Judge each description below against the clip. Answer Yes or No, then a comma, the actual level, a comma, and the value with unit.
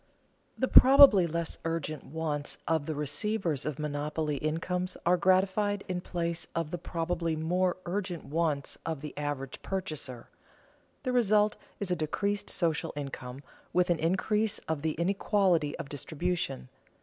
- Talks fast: No, average, 140 wpm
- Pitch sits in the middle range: Yes, medium, 165 Hz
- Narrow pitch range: No, average, 3.7 semitones